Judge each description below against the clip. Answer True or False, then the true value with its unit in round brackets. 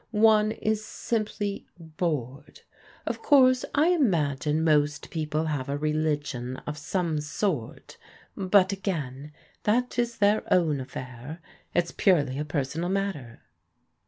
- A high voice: False (160 Hz)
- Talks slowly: True (125 wpm)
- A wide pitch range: True (5.7 semitones)